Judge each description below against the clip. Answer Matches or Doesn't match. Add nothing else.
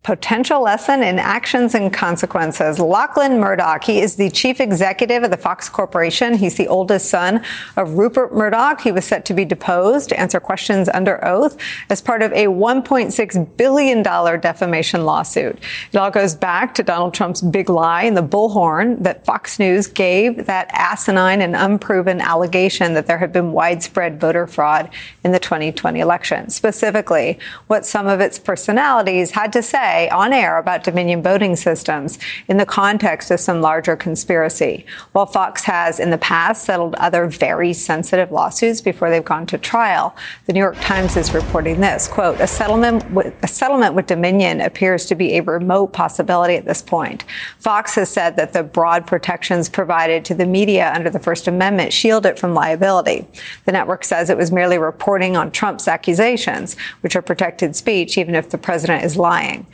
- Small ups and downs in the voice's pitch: Doesn't match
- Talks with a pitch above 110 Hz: Matches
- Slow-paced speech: Doesn't match